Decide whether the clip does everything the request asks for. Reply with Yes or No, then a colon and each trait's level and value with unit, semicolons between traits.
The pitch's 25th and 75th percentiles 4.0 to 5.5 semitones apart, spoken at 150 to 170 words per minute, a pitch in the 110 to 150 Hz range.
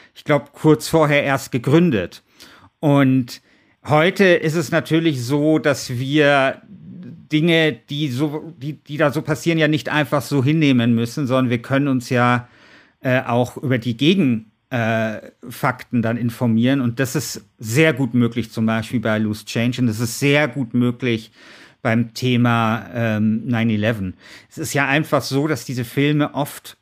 Yes: average, 4.3 semitones; average, 160 wpm; low, 135 Hz